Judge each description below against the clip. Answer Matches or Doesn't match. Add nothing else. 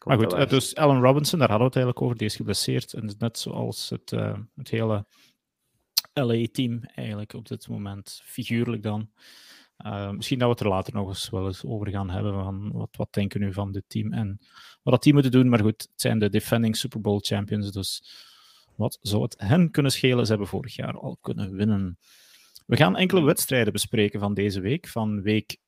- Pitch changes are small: Doesn't match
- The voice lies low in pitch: Matches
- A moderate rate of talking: Doesn't match